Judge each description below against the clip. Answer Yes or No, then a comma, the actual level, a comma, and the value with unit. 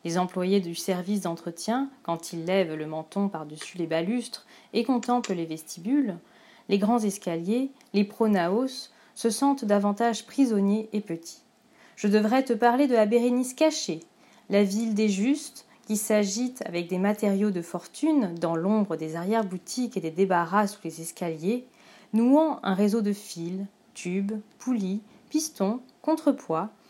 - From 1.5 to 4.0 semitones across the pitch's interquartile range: No, average, 4.8 semitones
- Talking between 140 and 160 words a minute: Yes, slow, 145 wpm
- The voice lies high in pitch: Yes, high, 210 Hz